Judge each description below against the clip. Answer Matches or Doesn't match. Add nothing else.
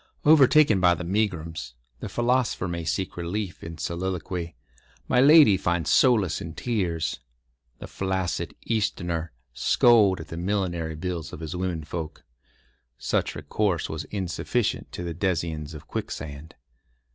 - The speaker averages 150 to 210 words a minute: Doesn't match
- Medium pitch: Doesn't match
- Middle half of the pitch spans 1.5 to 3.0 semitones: Doesn't match